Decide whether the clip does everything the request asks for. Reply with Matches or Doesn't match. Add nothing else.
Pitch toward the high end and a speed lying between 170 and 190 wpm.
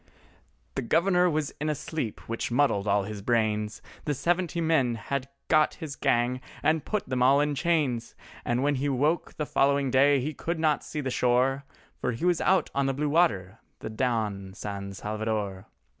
Doesn't match